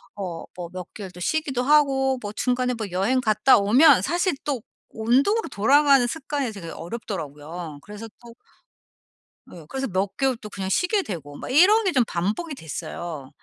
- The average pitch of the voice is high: Yes, high, 230 Hz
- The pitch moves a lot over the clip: Yes, wide, 6.9 semitones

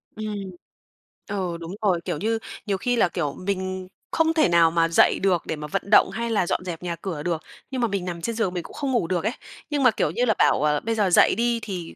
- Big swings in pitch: No, average, 4.9 semitones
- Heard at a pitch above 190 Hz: No, medium, 185 Hz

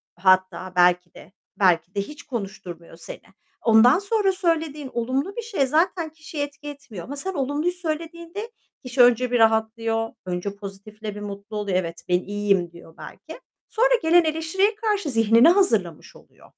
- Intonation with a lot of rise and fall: Yes, wide, 8.4 semitones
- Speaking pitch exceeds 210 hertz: Yes, high, 245 Hz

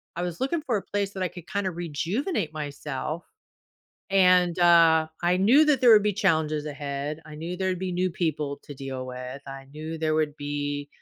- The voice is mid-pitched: Yes, medium, 165 Hz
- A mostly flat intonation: No, average, 4.2 semitones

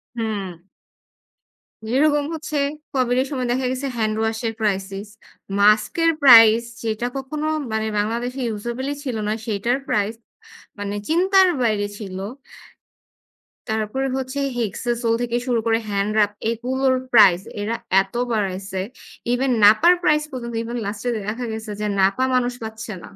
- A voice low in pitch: No, high, 230 Hz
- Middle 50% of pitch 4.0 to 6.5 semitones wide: No, average, 3.5 semitones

